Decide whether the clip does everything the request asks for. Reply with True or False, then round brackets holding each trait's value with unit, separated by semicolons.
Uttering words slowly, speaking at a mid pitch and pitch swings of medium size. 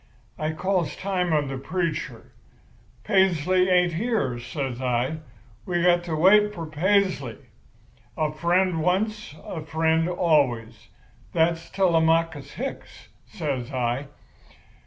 True (110 wpm; 165 Hz; 3.9 semitones)